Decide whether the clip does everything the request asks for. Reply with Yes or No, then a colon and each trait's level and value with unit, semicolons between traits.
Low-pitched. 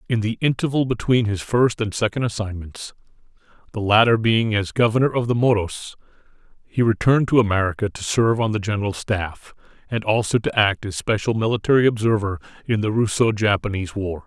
Yes: low, 110 Hz